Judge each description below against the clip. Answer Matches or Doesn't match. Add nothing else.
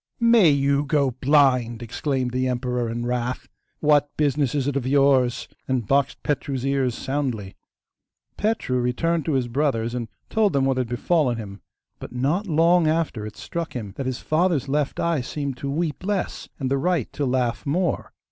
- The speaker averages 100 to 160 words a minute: Doesn't match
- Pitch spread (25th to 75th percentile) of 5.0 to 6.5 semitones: Doesn't match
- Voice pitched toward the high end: Doesn't match